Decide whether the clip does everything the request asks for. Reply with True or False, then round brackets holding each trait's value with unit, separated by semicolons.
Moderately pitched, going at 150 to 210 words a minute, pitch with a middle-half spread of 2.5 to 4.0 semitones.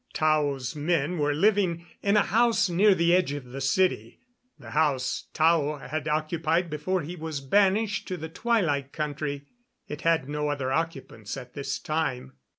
True (155 Hz; 160 wpm; 3.7 semitones)